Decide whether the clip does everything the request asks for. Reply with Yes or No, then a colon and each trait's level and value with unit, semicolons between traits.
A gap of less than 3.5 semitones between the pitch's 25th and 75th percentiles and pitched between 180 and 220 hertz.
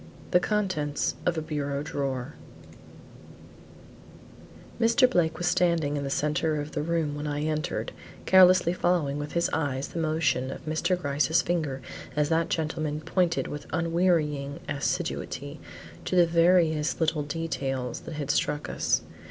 No: narrow, 2.6 semitones; medium, 155 Hz